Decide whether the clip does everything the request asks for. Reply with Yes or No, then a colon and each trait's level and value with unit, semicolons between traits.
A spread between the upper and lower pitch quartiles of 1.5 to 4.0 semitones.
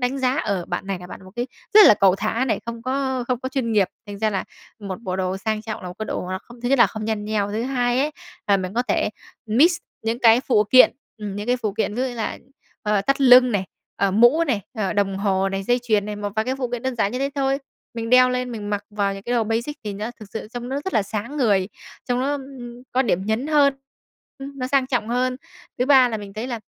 Yes: average, 3.7 semitones